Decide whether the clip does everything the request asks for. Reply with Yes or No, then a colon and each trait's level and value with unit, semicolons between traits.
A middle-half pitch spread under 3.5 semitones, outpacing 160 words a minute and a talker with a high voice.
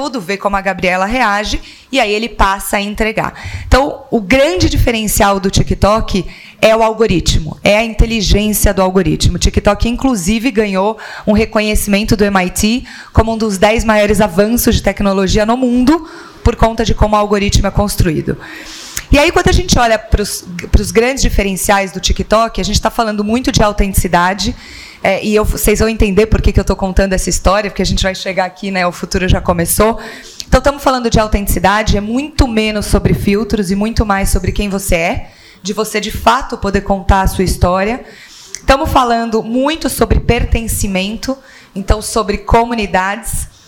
Yes: average, 2.8 semitones; average, 175 wpm; high, 215 Hz